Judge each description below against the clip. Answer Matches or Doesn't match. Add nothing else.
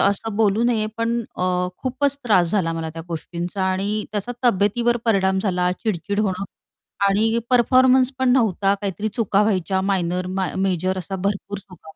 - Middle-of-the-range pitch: Doesn't match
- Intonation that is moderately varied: Matches